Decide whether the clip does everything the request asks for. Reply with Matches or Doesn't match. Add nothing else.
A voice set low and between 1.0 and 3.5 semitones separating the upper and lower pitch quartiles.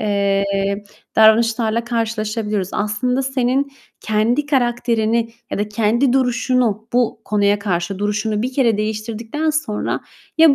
Doesn't match